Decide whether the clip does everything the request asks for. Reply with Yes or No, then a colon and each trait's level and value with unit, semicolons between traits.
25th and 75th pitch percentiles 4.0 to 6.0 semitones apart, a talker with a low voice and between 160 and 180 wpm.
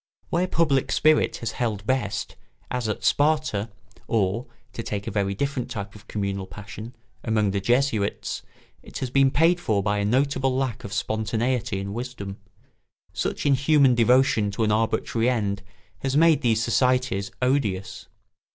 No: average, 4.5 semitones; low, 115 Hz; average, 150 wpm